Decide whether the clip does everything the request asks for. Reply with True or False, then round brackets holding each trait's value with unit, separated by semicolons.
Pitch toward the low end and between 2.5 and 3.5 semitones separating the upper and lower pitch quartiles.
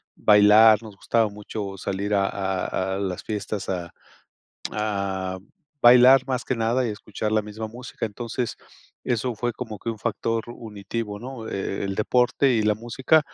True (110 Hz; 2.9 semitones)